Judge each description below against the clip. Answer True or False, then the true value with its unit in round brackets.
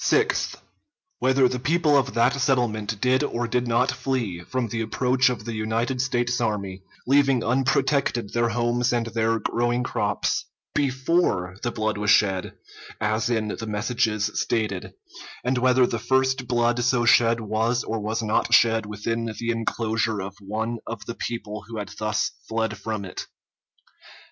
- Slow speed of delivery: False (160 wpm)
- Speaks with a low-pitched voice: True (115 Hz)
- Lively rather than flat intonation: False (2.5 semitones)